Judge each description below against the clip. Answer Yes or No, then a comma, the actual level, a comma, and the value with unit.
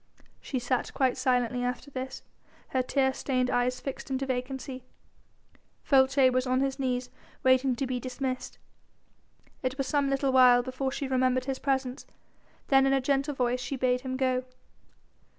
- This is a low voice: No, very high, 260 Hz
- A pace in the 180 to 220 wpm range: No, average, 160 wpm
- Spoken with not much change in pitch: Yes, narrow, 1.2 semitones